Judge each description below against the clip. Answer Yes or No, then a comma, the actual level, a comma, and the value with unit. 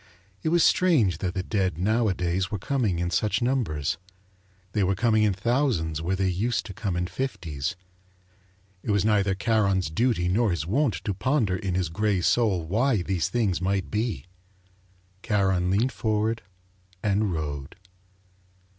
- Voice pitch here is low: Yes, low, 100 Hz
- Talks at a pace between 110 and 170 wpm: Yes, average, 155 wpm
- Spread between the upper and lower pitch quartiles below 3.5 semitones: No, average, 3.9 semitones